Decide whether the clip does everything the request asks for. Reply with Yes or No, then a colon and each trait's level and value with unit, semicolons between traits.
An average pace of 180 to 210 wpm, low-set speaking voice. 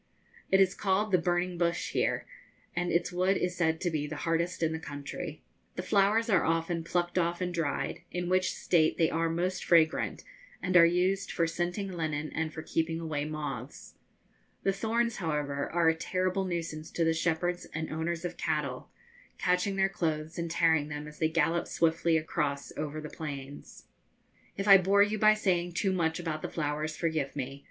No: average, 185 wpm; medium, 170 Hz